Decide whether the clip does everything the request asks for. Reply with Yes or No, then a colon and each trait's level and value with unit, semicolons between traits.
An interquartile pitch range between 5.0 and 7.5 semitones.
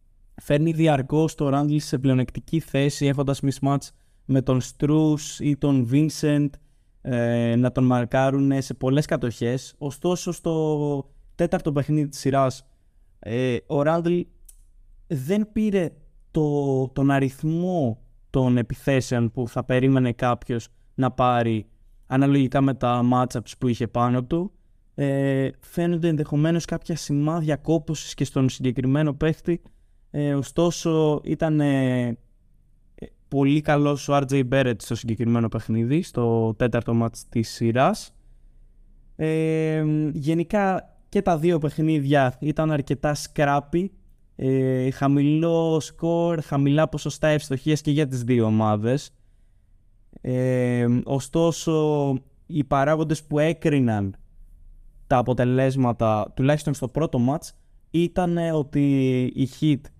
No: average, 4.0 semitones